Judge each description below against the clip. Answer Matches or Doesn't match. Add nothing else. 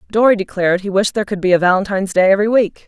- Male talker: Doesn't match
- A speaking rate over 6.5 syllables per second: Matches